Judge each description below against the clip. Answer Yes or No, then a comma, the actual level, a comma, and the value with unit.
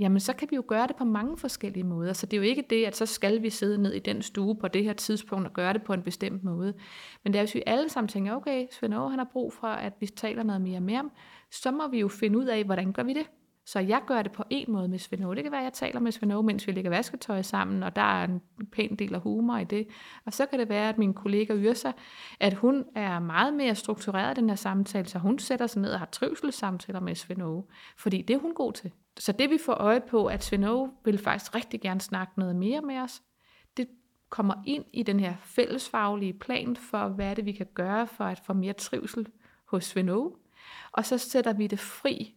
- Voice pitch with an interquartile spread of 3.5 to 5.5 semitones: Yes, average, 3.9 semitones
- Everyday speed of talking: No, fast, 255 wpm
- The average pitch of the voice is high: Yes, high, 215 Hz